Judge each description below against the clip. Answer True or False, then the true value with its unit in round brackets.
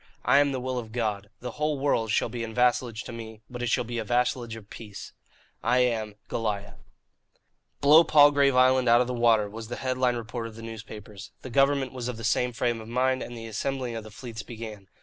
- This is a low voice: True (120 Hz)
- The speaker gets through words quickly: True (230 wpm)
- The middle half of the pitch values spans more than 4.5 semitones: False (2.4 semitones)